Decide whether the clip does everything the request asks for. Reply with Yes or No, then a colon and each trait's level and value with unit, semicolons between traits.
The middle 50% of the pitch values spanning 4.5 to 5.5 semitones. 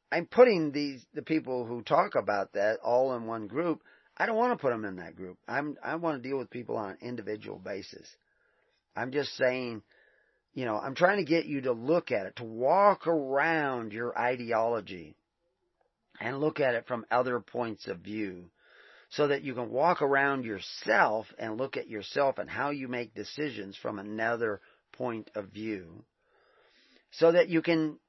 Yes: average, 5.1 semitones